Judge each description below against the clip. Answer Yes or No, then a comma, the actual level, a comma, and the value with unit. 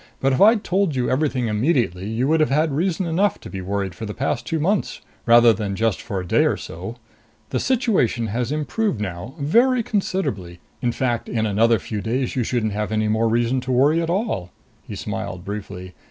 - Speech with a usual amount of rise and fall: No, wide, 6.9 semitones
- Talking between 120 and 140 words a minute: No, fast, 205 wpm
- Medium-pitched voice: No, low, 120 Hz